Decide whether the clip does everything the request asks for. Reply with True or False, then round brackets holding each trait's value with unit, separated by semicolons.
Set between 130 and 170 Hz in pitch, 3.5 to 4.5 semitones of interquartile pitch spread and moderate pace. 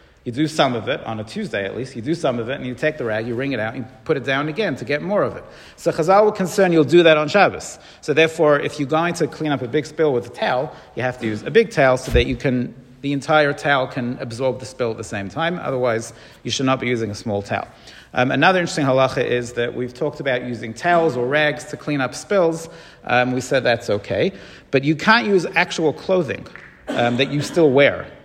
False (140 Hz; 4.2 semitones; 260 wpm)